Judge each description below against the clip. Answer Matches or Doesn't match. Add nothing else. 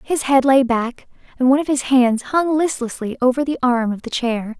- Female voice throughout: Matches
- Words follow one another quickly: Matches